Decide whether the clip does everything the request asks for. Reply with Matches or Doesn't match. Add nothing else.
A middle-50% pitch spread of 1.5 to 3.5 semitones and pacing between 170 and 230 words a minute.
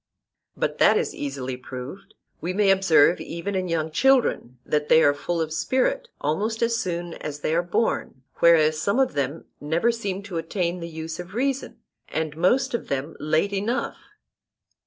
Doesn't match